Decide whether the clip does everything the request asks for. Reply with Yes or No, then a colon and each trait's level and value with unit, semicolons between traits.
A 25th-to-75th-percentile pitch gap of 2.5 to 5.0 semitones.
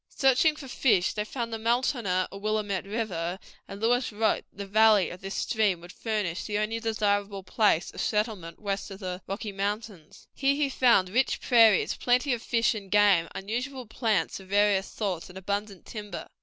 Yes: average, 2.9 semitones